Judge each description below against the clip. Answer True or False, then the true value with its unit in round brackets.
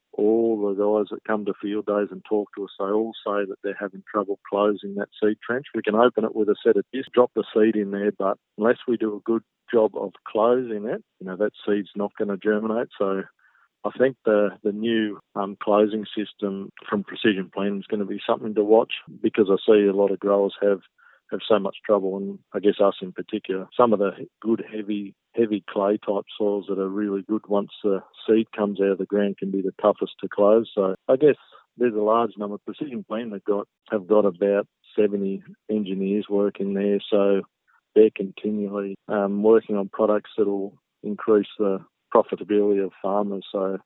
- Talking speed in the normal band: False (210 wpm)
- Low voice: True (105 Hz)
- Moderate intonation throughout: False (1.4 semitones)